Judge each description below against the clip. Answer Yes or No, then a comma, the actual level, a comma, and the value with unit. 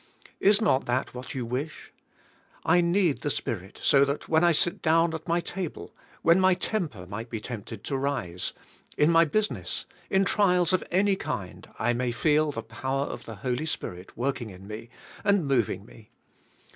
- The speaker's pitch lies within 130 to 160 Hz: Yes, medium, 140 Hz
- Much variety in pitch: Yes, wide, 6.5 semitones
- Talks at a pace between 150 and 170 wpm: No, average, 185 wpm